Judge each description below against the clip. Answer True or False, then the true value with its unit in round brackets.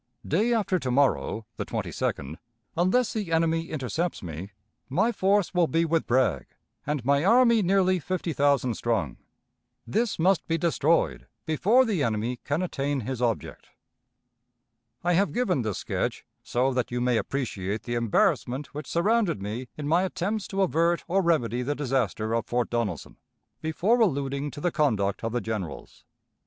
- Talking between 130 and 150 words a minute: False (160 wpm)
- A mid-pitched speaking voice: True (145 Hz)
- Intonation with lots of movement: True (6.9 semitones)